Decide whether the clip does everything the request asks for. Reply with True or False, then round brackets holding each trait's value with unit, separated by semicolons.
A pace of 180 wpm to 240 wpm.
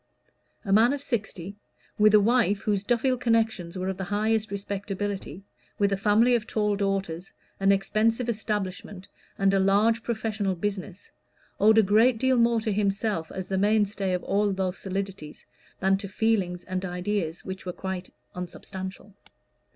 False (160 wpm)